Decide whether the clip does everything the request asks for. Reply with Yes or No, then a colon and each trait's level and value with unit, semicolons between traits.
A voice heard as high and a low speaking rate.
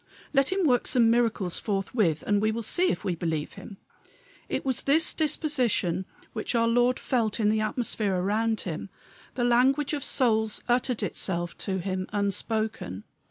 No: high, 220 Hz; average, 160 wpm